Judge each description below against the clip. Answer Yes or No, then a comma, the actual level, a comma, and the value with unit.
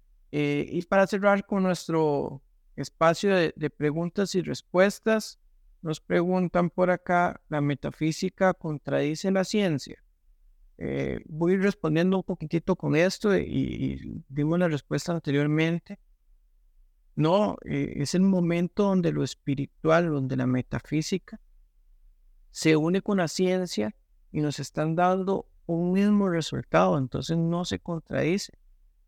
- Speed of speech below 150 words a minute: Yes, average, 130 wpm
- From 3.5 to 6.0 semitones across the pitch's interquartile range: Yes, average, 4.6 semitones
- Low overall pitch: No, medium, 165 Hz